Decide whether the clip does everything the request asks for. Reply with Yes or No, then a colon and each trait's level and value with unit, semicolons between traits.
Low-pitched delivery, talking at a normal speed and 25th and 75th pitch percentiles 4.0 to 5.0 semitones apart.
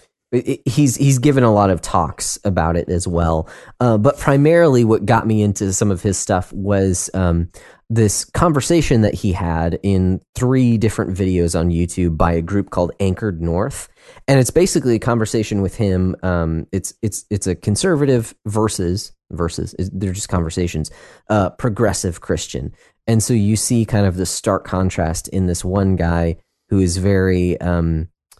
Yes: low, 100 Hz; average, 170 wpm; average, 4.3 semitones